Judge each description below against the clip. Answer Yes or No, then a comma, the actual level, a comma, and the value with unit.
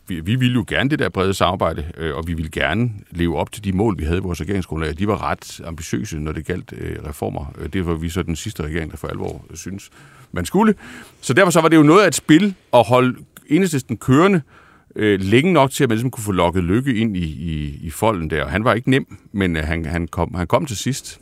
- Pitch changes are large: Yes, wide, 6.8 semitones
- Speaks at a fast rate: Yes, fast, 245 wpm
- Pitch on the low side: Yes, very low, 95 Hz